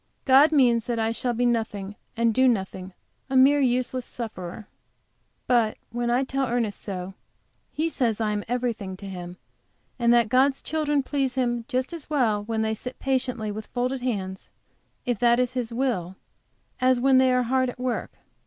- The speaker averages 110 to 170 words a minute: No, average, 180 wpm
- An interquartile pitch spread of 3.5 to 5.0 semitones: No, average, 2.9 semitones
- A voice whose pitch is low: No, high, 240 Hz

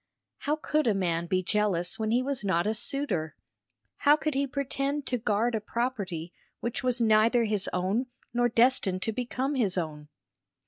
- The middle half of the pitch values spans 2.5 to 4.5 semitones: No, wide, 5.4 semitones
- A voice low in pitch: No, high, 225 Hz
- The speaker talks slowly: No, average, 175 wpm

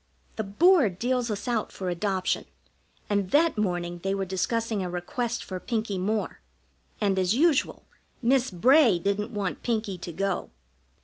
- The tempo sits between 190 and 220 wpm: No, average, 150 wpm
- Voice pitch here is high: Yes, high, 205 Hz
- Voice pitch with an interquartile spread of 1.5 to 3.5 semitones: No, average, 4.3 semitones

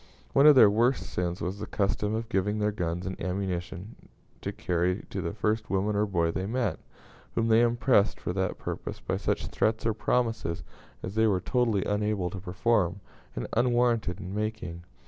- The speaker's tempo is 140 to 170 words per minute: No, average, 185 wpm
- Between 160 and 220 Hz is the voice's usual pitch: No, low, 105 Hz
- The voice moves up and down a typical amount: Yes, average, 3.5 semitones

